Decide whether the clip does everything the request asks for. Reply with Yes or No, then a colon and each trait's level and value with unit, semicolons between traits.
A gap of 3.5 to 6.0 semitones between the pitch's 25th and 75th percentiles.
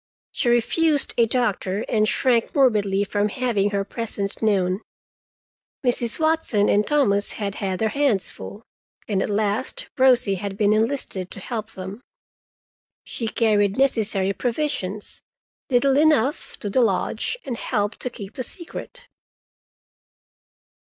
Yes: average, 3.9 semitones